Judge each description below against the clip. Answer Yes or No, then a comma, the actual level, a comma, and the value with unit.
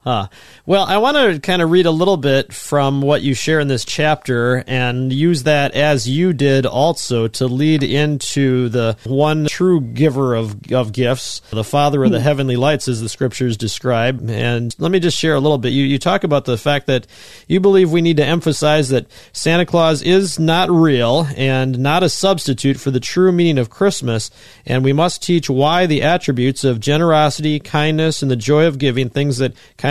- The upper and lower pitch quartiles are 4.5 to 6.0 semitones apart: No, average, 3.8 semitones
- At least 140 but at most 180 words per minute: No, average, 200 wpm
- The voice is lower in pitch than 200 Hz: Yes, medium, 140 Hz